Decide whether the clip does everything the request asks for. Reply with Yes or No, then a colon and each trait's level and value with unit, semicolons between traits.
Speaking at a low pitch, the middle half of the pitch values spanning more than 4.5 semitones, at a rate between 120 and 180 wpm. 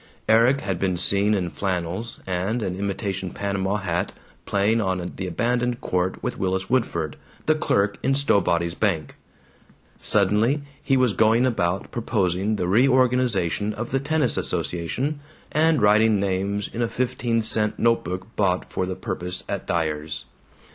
No: low, 100 Hz; average, 4.2 semitones; average, 150 wpm